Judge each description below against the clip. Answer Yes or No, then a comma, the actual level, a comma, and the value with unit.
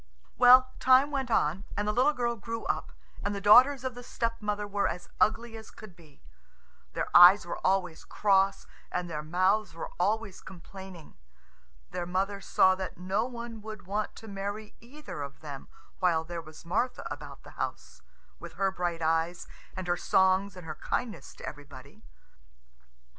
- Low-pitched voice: No, high, 195 Hz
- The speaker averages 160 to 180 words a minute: Yes, average, 170 wpm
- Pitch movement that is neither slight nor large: Yes, average, 4.2 semitones